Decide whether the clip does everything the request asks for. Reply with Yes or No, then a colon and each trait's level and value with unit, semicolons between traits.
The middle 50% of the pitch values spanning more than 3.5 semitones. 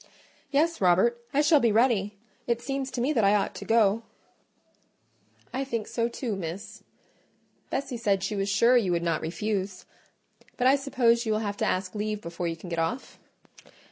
Yes: average, 4.1 semitones